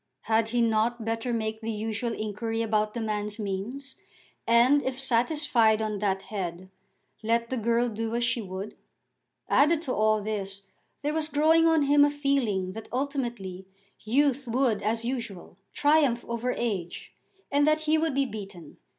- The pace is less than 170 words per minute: Yes, average, 160 wpm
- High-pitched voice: Yes, high, 230 Hz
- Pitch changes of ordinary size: Yes, average, 4.1 semitones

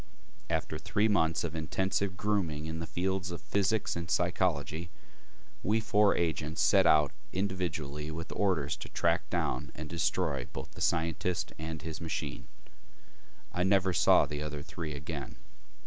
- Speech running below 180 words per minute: Yes, average, 150 wpm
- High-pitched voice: No, very low, 85 Hz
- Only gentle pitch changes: No, average, 3.4 semitones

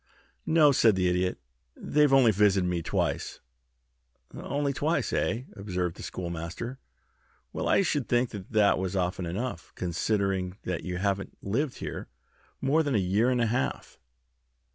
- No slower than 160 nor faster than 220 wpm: No, average, 145 wpm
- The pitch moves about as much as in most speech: No, wide, 5.9 semitones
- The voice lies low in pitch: Yes, low, 100 Hz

